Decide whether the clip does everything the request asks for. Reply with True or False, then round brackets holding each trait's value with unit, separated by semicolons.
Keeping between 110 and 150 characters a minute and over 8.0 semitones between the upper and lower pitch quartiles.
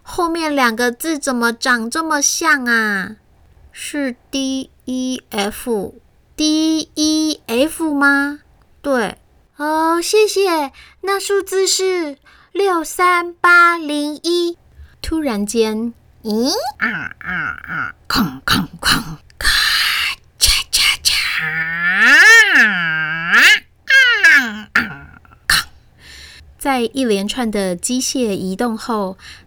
False (125 characters per minute; 6.5 semitones)